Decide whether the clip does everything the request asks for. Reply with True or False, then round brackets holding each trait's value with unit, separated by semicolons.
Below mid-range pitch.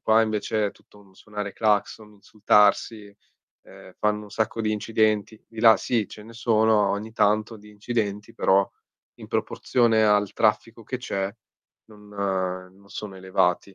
True (105 Hz)